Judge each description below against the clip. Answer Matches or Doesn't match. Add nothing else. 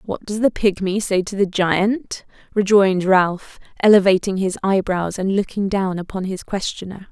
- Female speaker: Matches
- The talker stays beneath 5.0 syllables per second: Matches